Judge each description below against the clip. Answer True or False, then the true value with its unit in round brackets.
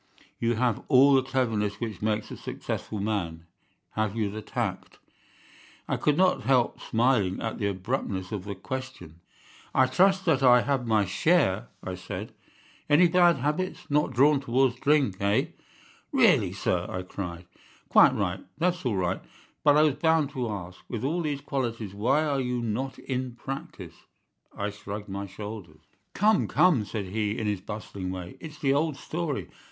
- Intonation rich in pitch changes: True (5.8 semitones)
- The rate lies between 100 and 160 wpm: False (170 wpm)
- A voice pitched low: True (115 Hz)